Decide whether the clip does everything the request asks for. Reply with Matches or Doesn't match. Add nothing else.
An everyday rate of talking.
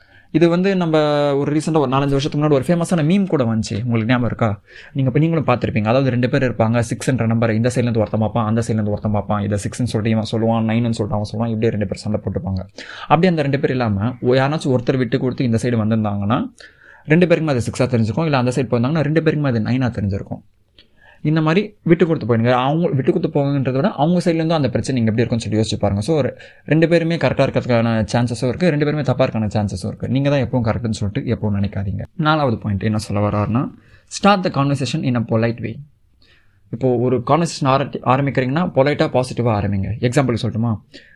Doesn't match